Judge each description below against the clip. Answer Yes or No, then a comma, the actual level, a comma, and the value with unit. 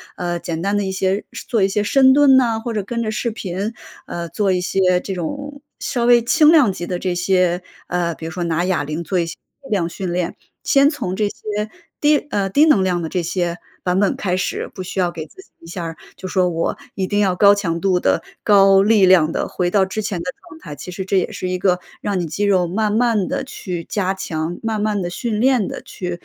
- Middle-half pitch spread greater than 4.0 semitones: No, average, 3.4 semitones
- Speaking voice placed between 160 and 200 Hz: Yes, high, 190 Hz